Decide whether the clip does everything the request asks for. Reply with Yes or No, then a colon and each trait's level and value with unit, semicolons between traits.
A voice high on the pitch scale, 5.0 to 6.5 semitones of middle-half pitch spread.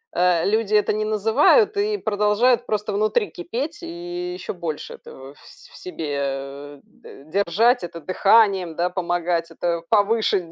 Yes: high, 200 Hz; average, 5.3 semitones